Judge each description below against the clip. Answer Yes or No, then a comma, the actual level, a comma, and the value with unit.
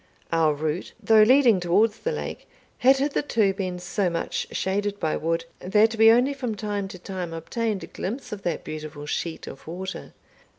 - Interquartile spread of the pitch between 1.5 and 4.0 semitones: No, average, 4.7 semitones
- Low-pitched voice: No, high, 195 Hz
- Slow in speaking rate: No, average, 175 wpm